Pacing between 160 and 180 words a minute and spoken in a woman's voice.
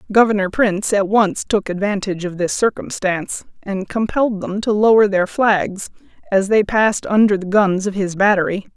Yes: average, 170 wpm; female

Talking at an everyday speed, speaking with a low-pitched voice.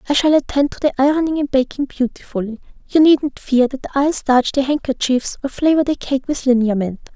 No: average, 185 wpm; very high, 270 Hz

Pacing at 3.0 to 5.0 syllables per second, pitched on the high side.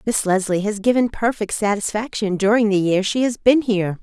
No: 5.4 syllables/s; high, 210 Hz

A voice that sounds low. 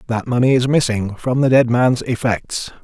Yes: low, 120 Hz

